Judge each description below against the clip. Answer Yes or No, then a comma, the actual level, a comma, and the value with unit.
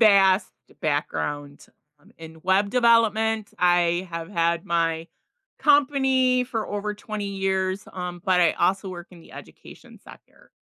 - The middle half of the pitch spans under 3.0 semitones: No, average, 4.1 semitones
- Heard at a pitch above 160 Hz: Yes, high, 190 Hz